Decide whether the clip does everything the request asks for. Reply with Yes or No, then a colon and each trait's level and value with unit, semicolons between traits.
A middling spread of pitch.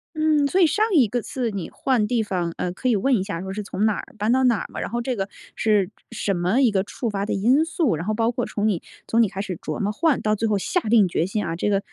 Yes: average, 4.1 semitones